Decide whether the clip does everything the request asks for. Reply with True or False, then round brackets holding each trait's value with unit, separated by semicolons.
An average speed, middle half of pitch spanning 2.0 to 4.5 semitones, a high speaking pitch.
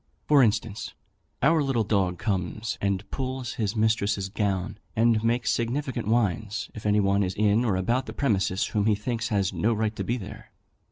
False (180 wpm; 3.0 semitones; 110 Hz)